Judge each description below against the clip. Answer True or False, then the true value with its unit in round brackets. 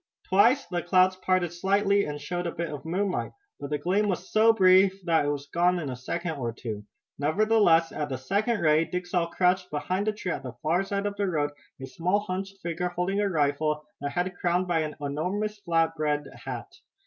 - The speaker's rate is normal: False (210 wpm)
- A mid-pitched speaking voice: True (175 Hz)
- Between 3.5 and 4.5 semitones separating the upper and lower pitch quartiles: True (4.1 semitones)